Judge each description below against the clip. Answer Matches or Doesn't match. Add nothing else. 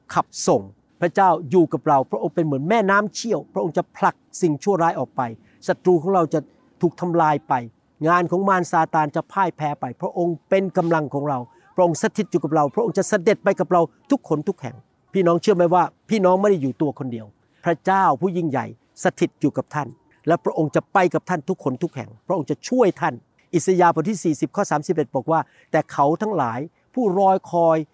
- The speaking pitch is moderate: Matches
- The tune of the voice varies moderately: Matches